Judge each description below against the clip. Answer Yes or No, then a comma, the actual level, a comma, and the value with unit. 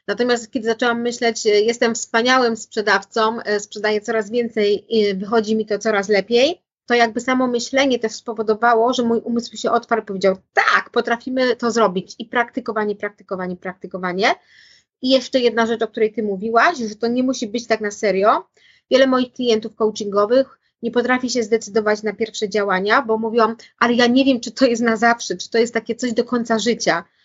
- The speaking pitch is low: No, high, 230 Hz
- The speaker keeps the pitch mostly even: Yes, narrow, 2.1 semitones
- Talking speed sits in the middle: No, fast, 185 wpm